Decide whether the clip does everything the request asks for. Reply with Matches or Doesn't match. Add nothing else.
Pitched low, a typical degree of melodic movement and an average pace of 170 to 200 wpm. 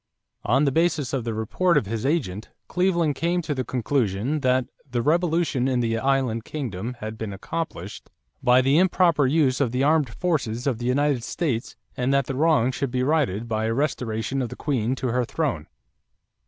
Matches